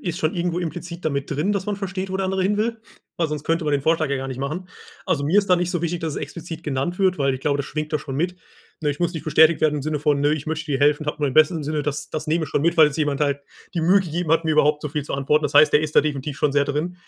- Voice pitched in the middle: Yes, medium, 155 Hz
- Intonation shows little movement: No, average, 3.0 semitones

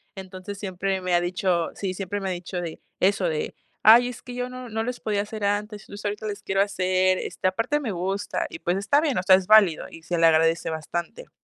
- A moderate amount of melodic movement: Yes, average, 3.0 semitones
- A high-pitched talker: Yes, high, 195 Hz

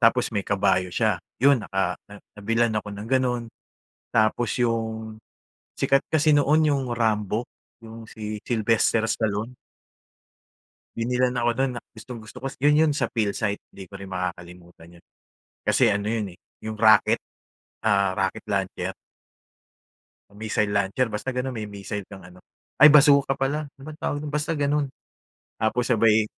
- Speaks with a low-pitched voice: Yes, low, 110 Hz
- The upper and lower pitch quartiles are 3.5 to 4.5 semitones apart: Yes, average, 4.0 semitones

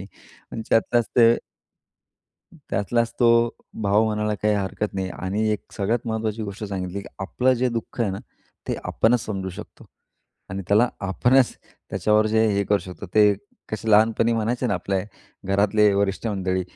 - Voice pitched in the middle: No, low, 105 Hz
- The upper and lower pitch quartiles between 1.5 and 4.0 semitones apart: Yes, narrow, 2.5 semitones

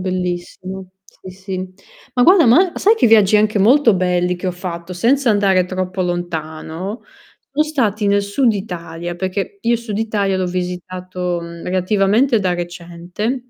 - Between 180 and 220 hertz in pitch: Yes, high, 190 Hz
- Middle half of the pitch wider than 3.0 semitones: Yes, average, 3.4 semitones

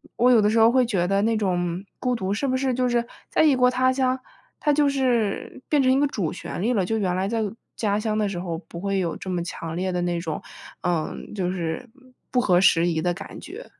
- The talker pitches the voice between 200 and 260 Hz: Yes, high, 205 Hz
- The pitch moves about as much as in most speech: No, wide, 5.9 semitones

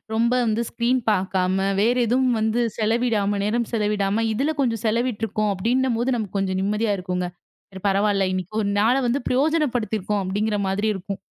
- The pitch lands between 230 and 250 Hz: No, high, 215 Hz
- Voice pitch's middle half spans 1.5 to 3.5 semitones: Yes, average, 3.2 semitones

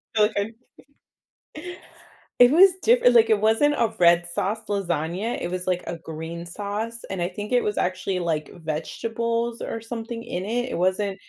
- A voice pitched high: Yes, high, 205 Hz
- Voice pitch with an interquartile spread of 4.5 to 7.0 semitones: Yes, average, 4.8 semitones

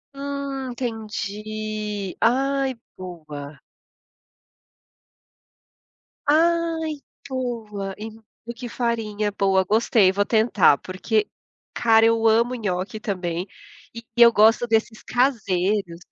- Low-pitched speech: No, high, 220 Hz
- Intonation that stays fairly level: No, average, 3.5 semitones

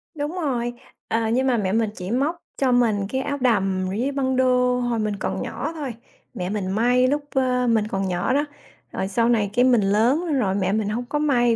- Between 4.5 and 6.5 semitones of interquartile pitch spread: No, average, 3.9 semitones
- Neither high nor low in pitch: No, high, 240 Hz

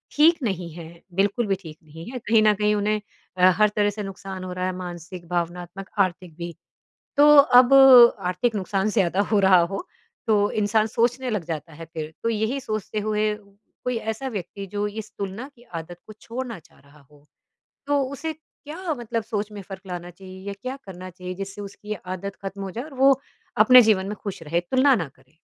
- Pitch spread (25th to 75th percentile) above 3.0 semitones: Yes, average, 3.8 semitones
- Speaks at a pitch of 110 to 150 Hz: No, high, 200 Hz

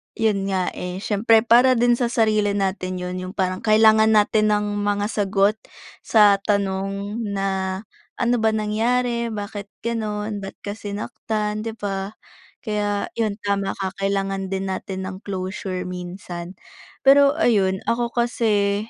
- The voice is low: No, high, 205 Hz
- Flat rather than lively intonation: Yes, narrow, 2.1 semitones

